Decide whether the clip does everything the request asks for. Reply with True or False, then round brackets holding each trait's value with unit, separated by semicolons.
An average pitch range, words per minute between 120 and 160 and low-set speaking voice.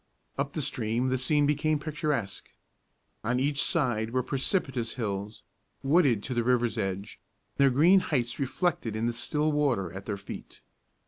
True (4.7 semitones; 155 wpm; 130 Hz)